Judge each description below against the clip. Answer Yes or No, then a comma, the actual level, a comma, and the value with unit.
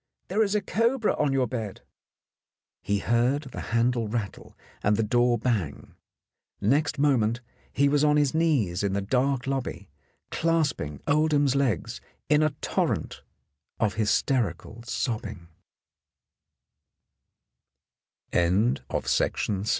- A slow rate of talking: Yes, slow, 110 wpm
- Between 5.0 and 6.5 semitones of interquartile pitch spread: Yes, average, 5.3 semitones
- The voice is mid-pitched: No, low, 125 Hz